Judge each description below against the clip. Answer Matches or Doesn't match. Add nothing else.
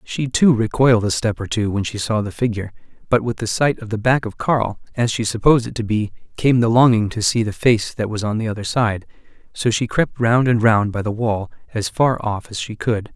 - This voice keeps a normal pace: Doesn't match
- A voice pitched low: Matches